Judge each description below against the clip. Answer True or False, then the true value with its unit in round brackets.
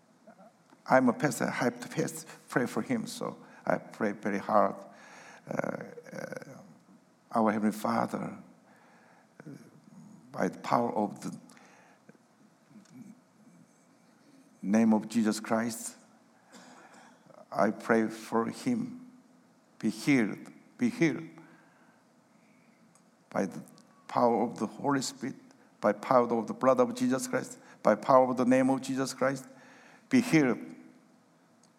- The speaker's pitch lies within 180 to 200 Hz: False (135 Hz)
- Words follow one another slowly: True (115 wpm)